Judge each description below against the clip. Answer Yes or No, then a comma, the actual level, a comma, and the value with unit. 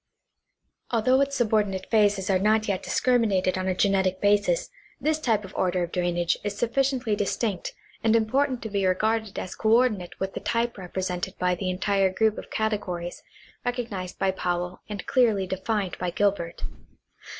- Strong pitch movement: No, average, 3.3 semitones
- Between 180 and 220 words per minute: No, average, 160 wpm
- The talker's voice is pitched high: Yes, high, 205 Hz